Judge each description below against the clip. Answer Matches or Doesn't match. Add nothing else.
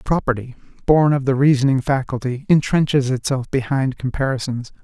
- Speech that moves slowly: Matches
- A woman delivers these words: Doesn't match